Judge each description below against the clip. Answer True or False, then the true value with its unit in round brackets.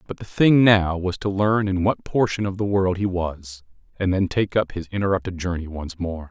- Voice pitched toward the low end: True (95 Hz)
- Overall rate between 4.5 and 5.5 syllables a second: True (5.0 syllables/s)